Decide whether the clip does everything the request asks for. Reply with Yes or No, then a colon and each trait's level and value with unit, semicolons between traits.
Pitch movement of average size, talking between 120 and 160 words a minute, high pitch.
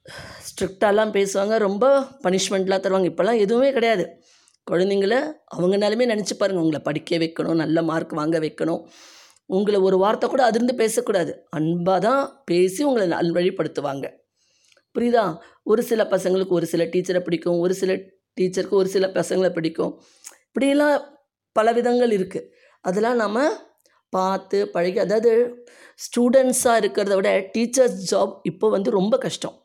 Yes: average, 4.6 semitones; average, 125 wpm; high, 200 Hz